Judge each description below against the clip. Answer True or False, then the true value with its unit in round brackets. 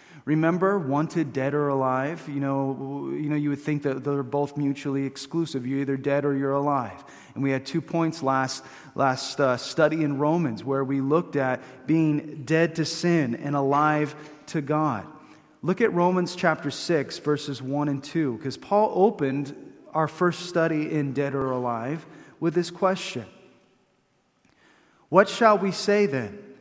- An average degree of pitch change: True (3.1 semitones)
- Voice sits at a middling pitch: True (145 Hz)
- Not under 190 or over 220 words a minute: False (160 wpm)